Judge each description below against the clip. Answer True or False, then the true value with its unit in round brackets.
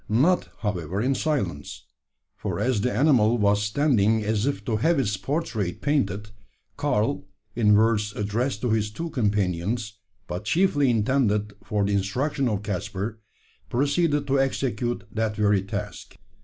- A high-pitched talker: False (110 Hz)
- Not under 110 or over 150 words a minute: True (140 wpm)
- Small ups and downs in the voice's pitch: False (4.7 semitones)